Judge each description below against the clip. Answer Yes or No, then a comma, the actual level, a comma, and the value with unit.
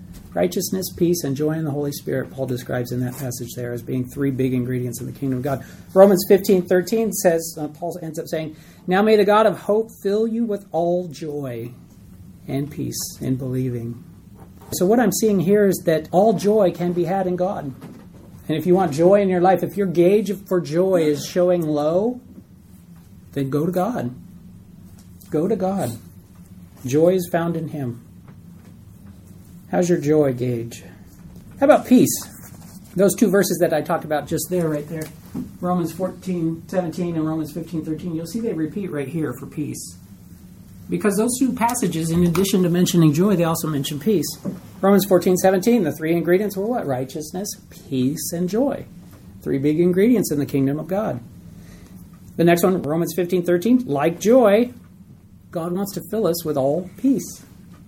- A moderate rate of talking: Yes, average, 175 wpm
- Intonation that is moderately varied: No, wide, 6.0 semitones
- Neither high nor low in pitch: Yes, medium, 165 Hz